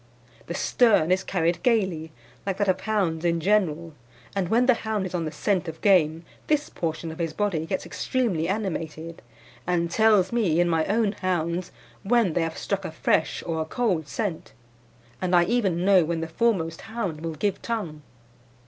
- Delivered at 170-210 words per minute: Yes, average, 185 wpm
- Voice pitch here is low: No, medium, 180 Hz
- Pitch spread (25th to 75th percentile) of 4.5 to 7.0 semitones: No, average, 4.1 semitones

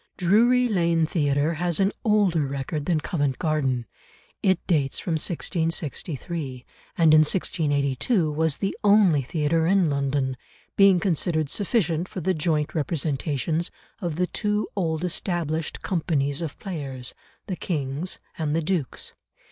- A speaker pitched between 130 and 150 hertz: No, medium, 160 Hz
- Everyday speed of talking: No, slow, 130 wpm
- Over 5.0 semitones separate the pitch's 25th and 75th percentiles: No, average, 3.7 semitones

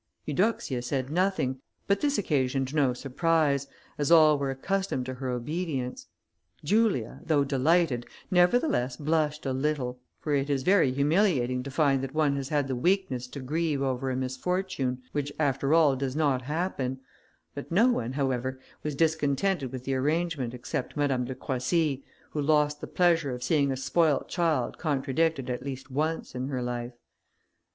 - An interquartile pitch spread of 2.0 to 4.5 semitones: Yes, average, 3.6 semitones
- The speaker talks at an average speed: Yes, average, 160 wpm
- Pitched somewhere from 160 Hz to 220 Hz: No, medium, 140 Hz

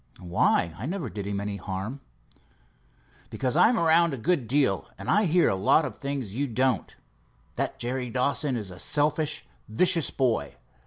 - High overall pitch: No, low, 130 Hz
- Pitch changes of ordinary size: No, wide, 6.8 semitones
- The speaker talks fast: No, average, 165 wpm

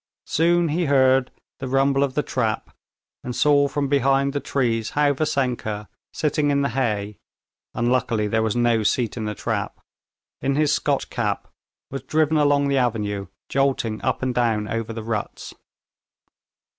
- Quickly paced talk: No, average, 155 wpm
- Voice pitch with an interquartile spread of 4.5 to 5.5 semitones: No, average, 3.9 semitones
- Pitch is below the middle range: Yes, low, 130 Hz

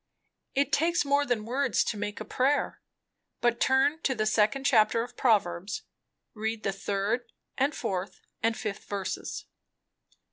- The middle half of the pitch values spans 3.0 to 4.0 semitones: No, average, 4.4 semitones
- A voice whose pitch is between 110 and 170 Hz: No, high, 225 Hz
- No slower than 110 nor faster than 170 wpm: Yes, average, 150 wpm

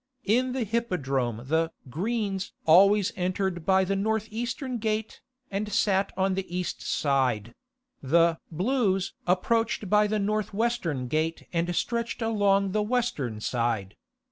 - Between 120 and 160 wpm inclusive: Yes, slow, 135 wpm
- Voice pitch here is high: Yes, high, 195 Hz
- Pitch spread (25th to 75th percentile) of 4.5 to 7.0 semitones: Yes, average, 5.0 semitones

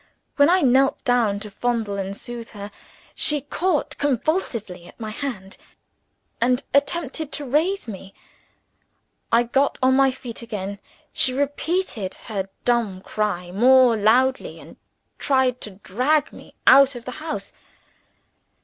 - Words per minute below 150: Yes, slow, 135 wpm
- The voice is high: Yes, high, 245 Hz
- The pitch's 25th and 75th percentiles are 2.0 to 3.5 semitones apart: No, average, 4.9 semitones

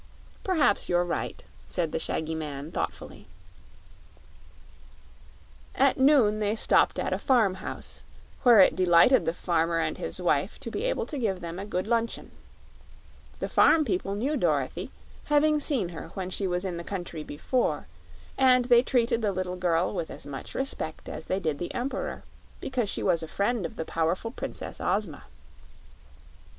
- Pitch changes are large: Yes, wide, 6.5 semitones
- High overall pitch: Yes, high, 195 Hz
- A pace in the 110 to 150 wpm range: No, average, 165 wpm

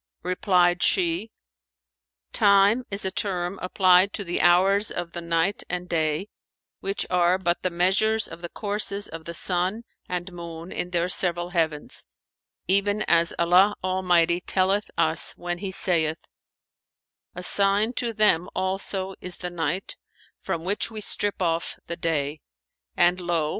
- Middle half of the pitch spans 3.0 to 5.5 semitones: No, narrow, 2.5 semitones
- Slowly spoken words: No, average, 145 wpm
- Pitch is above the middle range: No, medium, 180 Hz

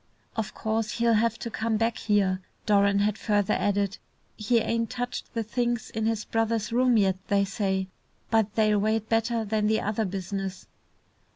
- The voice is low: No, high, 215 Hz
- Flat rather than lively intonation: Yes, narrow, 2.0 semitones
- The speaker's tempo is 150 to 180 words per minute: Yes, average, 170 wpm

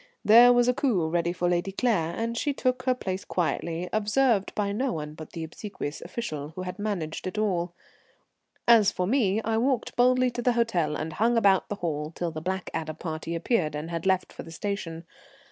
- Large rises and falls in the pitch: Yes, wide, 5.8 semitones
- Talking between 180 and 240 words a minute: Yes, average, 200 wpm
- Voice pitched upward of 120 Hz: Yes, high, 190 Hz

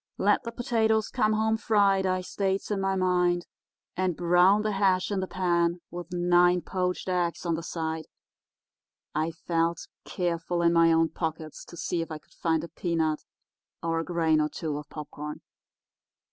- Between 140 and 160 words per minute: No, average, 175 wpm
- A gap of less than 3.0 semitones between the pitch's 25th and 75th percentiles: Yes, narrow, 2.4 semitones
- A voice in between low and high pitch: Yes, medium, 175 Hz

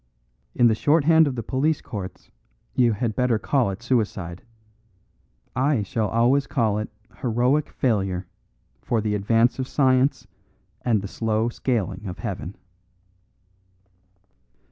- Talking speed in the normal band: No, slow, 130 wpm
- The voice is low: Yes, low, 115 Hz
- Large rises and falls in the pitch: No, average, 3.8 semitones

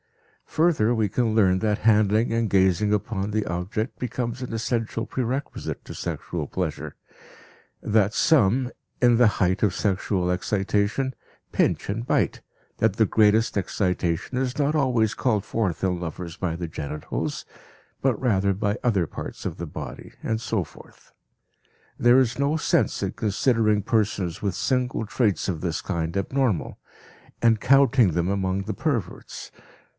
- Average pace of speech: Yes, average, 150 wpm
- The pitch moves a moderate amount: Yes, average, 4.2 semitones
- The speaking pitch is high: No, low, 105 Hz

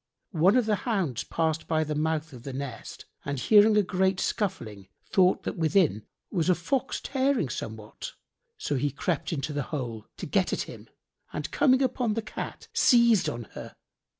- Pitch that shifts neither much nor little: No, wide, 7.1 semitones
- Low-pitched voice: No, medium, 165 Hz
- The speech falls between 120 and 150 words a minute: No, average, 180 wpm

